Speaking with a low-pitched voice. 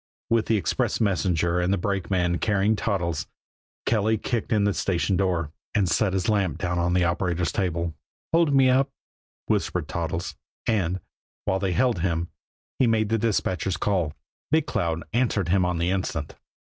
Yes: very low, 95 Hz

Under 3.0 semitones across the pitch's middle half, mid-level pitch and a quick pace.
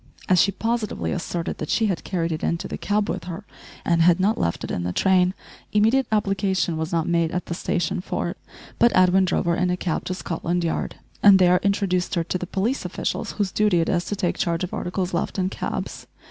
Yes: narrow, 2.6 semitones; medium, 180 Hz; fast, 230 wpm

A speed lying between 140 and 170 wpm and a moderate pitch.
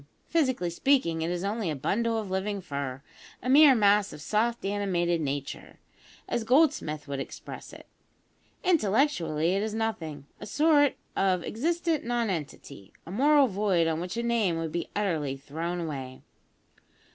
No: average, 150 wpm; high, 195 Hz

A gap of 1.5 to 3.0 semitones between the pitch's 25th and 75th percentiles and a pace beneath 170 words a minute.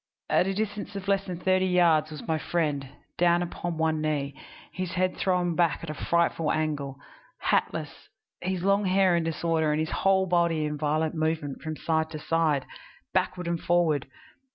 No: average, 2.7 semitones; average, 175 wpm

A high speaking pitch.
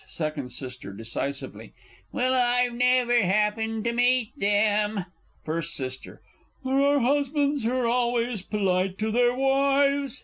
Yes: high, 235 Hz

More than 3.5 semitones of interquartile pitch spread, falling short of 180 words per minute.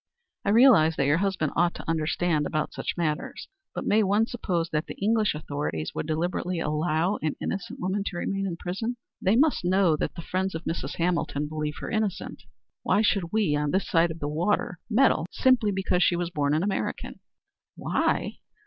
No: average, 4.3 semitones; average, 190 wpm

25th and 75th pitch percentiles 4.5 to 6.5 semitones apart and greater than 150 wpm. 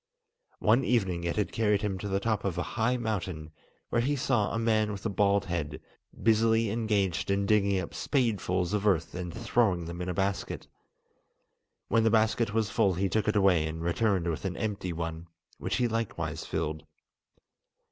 No: average, 4.0 semitones; average, 185 wpm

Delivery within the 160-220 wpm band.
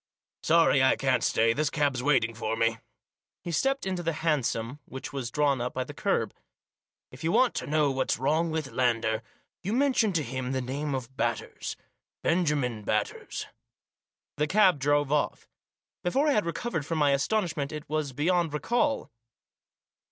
Yes: average, 170 wpm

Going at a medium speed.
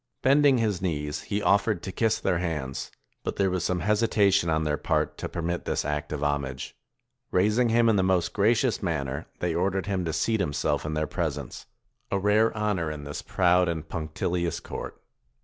Yes: average, 190 wpm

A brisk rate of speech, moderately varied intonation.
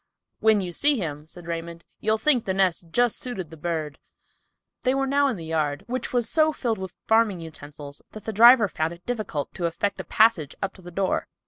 No: fast, 215 wpm; wide, 6.0 semitones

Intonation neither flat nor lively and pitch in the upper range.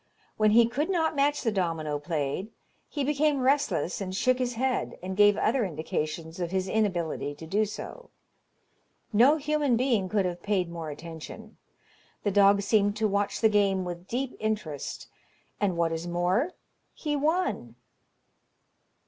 No: wide, 6.4 semitones; high, 205 Hz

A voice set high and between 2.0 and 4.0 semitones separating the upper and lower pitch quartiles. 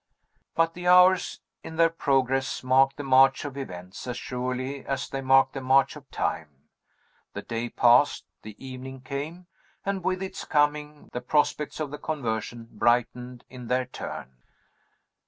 No: low, 135 Hz; average, 3.2 semitones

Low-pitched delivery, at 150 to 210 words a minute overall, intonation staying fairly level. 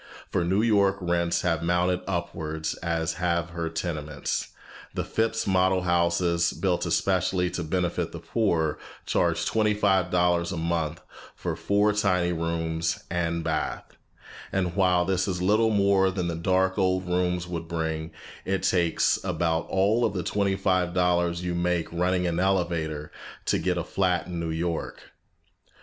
Yes: very low, 90 Hz; average, 160 wpm; narrow, 2.1 semitones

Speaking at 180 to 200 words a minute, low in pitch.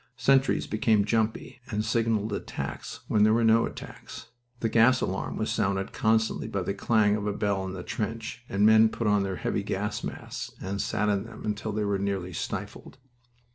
Yes: average, 190 wpm; low, 105 Hz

